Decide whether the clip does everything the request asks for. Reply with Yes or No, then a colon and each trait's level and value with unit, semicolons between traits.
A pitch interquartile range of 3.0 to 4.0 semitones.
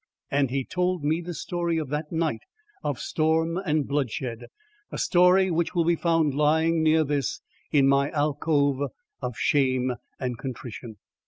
Yes: average, 3.3 semitones